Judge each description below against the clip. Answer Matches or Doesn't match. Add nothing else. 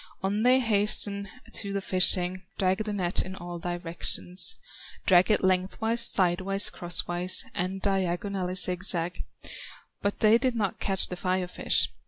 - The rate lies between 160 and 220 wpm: Doesn't match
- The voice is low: Doesn't match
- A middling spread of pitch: Doesn't match